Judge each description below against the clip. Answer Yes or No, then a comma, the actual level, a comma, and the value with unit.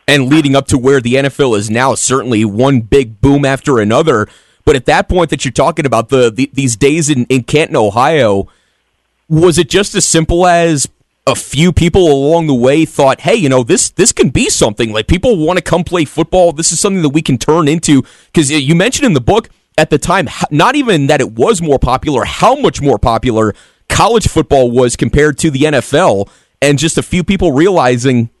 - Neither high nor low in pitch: Yes, medium, 145 Hz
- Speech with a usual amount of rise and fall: Yes, average, 3.9 semitones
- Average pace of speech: No, fast, 210 wpm